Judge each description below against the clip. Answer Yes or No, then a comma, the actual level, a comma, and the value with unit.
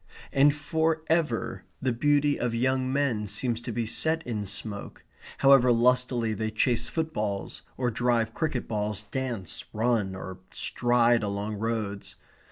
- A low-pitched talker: Yes, low, 120 Hz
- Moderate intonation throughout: Yes, average, 3.6 semitones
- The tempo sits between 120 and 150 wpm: Yes, average, 140 wpm